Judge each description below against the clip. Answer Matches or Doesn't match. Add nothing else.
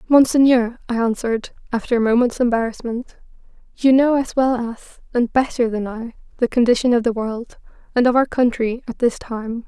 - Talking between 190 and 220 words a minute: Doesn't match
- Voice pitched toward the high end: Matches